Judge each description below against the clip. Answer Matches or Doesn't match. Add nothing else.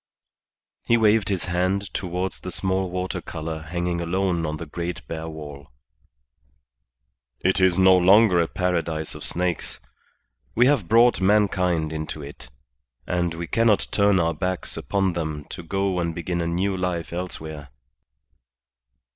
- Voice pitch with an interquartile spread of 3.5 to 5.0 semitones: Doesn't match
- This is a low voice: Matches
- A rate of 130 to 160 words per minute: Matches